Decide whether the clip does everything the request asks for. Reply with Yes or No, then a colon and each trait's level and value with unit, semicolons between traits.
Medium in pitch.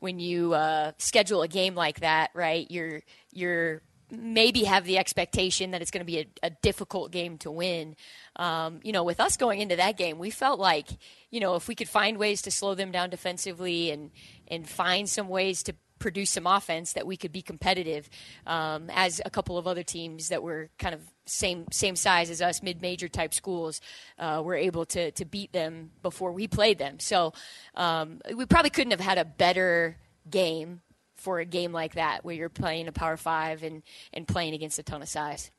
Yes: medium, 175 Hz